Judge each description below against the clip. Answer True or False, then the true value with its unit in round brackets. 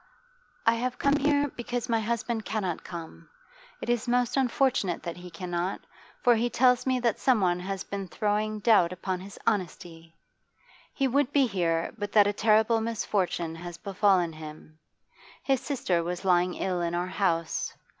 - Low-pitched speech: False (205 Hz)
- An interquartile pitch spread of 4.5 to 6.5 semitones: True (5.3 semitones)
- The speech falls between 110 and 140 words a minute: False (165 wpm)